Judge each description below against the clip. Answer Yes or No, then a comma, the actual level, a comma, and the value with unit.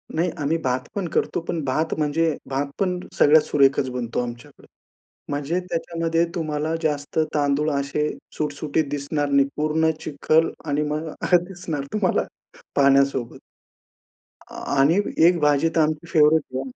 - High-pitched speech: No, medium, 150 Hz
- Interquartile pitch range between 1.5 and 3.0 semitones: Yes, narrow, 2.6 semitones